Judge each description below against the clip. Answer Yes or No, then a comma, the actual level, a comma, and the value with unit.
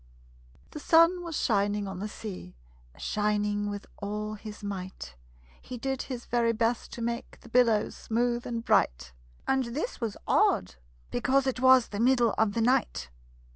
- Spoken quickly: No, average, 160 wpm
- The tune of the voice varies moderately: Yes, average, 3.3 semitones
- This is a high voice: Yes, high, 230 Hz